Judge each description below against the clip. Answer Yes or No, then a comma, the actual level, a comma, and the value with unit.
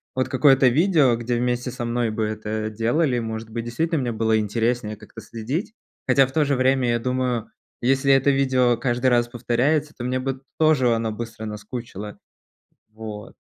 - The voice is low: Yes, low, 120 Hz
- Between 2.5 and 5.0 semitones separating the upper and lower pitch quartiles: Yes, average, 2.9 semitones